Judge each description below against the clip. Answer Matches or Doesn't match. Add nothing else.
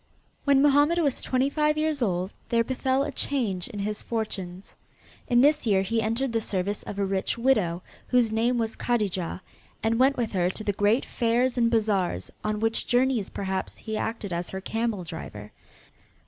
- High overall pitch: Matches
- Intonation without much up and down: Doesn't match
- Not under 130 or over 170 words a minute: Doesn't match